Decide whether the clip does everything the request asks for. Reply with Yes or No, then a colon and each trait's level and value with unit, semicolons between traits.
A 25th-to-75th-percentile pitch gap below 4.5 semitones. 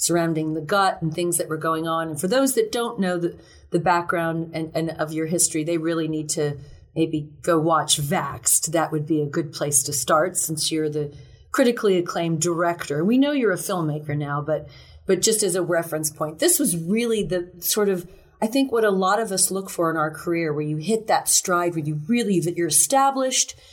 Yes: average, 3.4 semitones